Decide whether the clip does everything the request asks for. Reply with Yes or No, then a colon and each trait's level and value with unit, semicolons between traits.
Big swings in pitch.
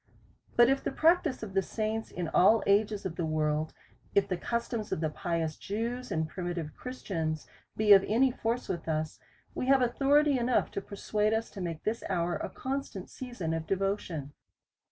Yes: wide, 6.1 semitones